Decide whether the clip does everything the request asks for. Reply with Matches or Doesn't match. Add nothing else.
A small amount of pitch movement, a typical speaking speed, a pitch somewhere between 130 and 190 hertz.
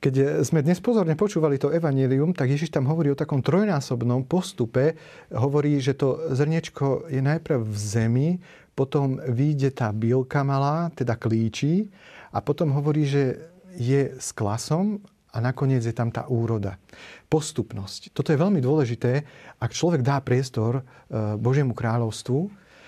Doesn't match